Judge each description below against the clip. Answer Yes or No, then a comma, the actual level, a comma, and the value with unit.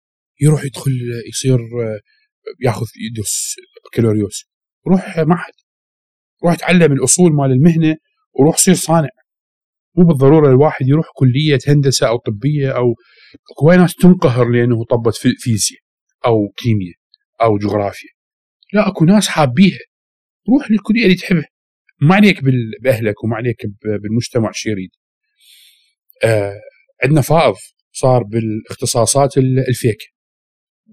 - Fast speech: No, average, 115 wpm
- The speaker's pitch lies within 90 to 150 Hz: Yes, medium, 140 Hz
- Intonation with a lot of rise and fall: Yes, wide, 7.6 semitones